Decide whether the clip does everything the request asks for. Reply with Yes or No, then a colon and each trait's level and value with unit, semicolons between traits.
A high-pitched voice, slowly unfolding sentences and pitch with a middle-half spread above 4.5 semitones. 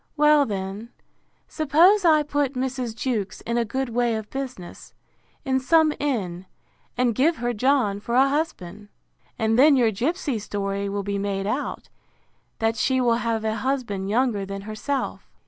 No: high, 240 Hz; average, 160 wpm; average, 5.0 semitones